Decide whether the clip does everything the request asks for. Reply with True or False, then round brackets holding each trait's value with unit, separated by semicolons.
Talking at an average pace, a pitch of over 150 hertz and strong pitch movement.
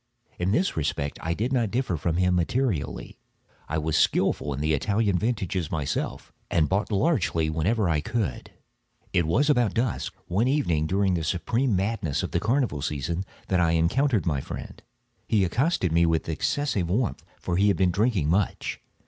False (175 wpm; 95 Hz; 5.8 semitones)